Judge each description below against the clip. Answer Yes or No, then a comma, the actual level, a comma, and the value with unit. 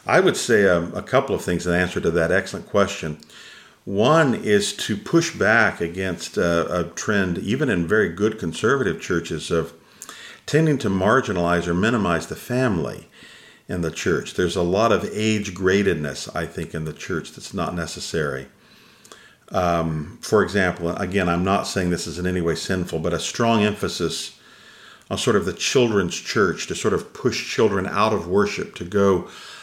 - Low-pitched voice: Yes, very low, 90 Hz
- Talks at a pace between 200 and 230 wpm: No, average, 175 wpm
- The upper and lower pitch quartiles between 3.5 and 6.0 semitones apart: No, average, 2.9 semitones